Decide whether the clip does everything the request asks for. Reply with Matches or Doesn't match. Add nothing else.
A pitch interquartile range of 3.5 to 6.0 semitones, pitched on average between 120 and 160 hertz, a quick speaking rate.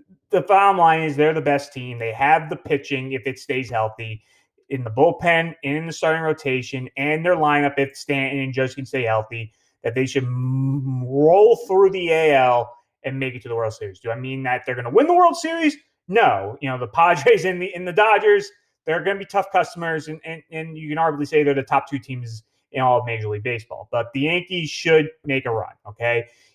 Matches